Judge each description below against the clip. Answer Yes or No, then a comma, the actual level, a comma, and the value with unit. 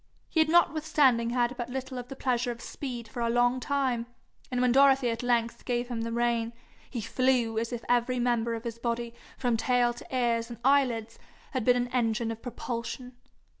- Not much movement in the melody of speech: Yes, narrow, 1.5 semitones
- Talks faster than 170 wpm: Yes, average, 200 wpm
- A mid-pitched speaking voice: No, high, 245 Hz